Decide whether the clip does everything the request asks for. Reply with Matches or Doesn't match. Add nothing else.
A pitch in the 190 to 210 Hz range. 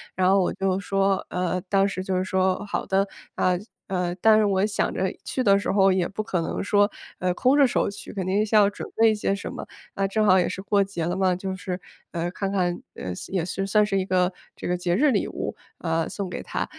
Matches